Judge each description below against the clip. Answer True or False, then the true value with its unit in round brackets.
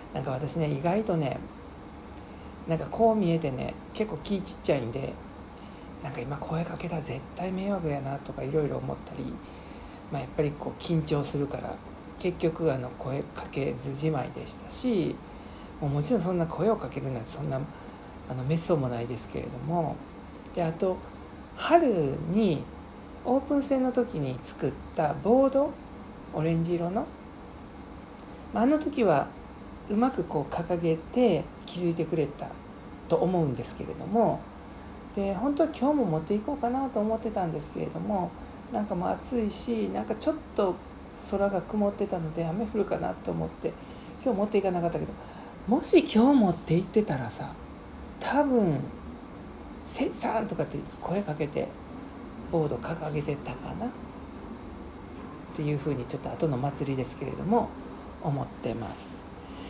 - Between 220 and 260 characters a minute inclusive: False (305 characters per minute)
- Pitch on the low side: False (170 Hz)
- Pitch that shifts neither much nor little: False (6.8 semitones)